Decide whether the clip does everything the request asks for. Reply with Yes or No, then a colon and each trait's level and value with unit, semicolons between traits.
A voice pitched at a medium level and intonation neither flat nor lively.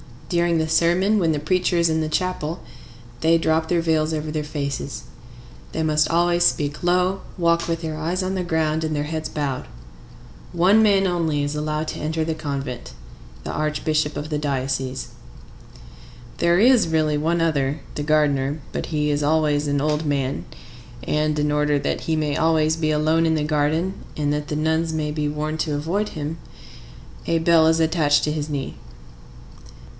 No: medium, 155 Hz; narrow, 1.9 semitones